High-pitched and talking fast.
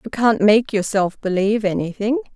No: high, 215 Hz; average, 155 wpm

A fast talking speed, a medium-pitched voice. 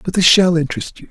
Yes: fast, 270 wpm; medium, 165 Hz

